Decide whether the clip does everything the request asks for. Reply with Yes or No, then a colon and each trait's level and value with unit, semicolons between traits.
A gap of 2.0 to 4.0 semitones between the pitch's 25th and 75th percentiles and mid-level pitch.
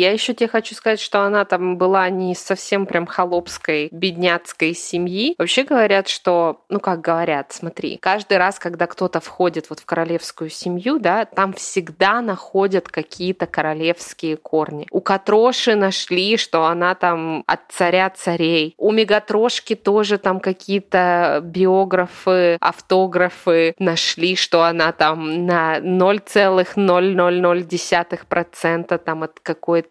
Yes: narrow, 2.5 semitones; medium, 180 Hz